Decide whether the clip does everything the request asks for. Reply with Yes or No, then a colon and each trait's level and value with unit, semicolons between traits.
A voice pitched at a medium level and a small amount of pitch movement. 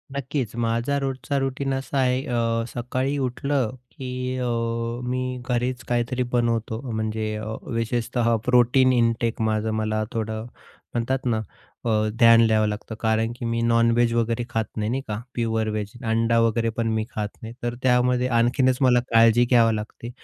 No: low, 115 Hz; narrow, 2.0 semitones